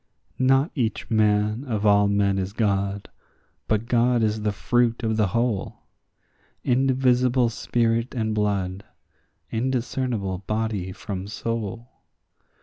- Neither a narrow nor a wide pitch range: Yes, average, 3.0 semitones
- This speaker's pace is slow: Yes, slow, 115 wpm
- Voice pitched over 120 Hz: No, low, 110 Hz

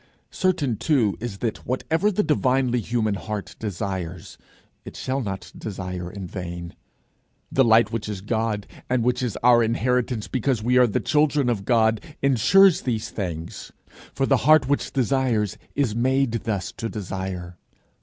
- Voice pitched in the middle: No, low, 115 Hz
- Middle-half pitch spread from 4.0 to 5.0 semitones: Yes, average, 4.5 semitones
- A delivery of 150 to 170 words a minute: Yes, average, 155 wpm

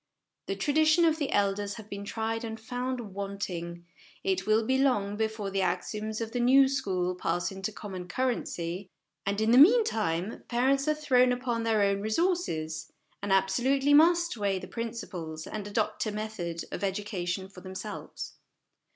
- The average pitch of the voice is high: Yes, high, 215 Hz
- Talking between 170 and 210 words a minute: No, average, 160 wpm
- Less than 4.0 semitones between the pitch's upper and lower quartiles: No, average, 4.5 semitones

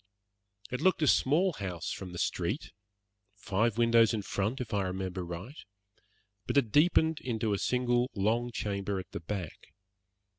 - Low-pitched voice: Yes, low, 110 Hz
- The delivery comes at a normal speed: Yes, average, 155 wpm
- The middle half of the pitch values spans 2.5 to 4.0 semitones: No, average, 4.5 semitones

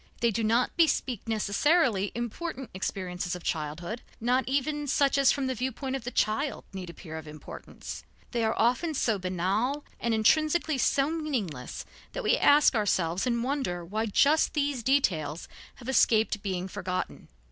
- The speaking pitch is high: Yes, high, 235 Hz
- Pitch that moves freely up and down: Yes, wide, 6.5 semitones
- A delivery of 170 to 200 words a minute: No, average, 160 wpm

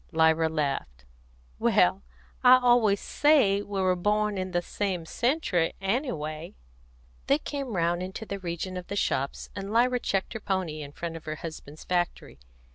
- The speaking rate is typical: Yes, average, 160 wpm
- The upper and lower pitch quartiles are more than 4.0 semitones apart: Yes, average, 4.6 semitones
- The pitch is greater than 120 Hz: Yes, medium, 185 Hz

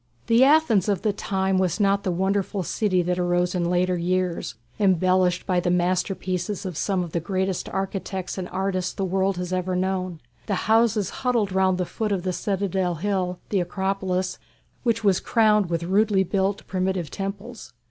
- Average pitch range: No, narrow, 1.8 semitones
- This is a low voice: No, high, 190 Hz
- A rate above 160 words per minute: Yes, average, 175 wpm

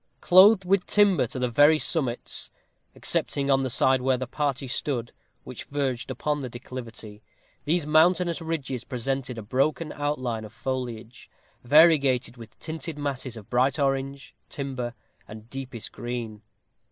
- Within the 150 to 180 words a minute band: No, average, 140 wpm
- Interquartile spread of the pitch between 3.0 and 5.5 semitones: Yes, average, 3.5 semitones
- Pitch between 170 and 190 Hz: No, low, 135 Hz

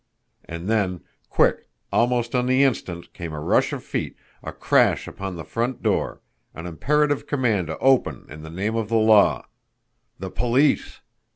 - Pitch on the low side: Yes, low, 110 Hz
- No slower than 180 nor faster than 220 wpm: No, average, 165 wpm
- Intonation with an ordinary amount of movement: No, wide, 6.4 semitones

